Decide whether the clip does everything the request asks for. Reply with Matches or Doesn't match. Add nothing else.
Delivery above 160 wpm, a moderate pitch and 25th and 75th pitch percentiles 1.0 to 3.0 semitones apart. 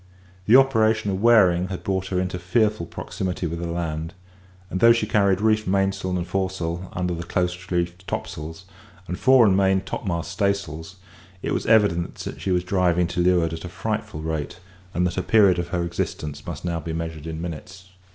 Doesn't match